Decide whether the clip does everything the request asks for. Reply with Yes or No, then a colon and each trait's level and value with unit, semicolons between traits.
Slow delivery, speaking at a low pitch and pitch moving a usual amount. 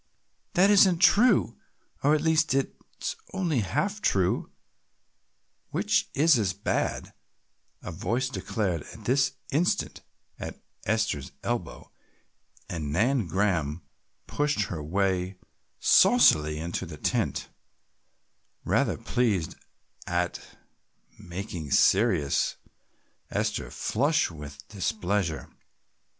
No: slow, 100 wpm; low, 100 Hz; wide, 8.4 semitones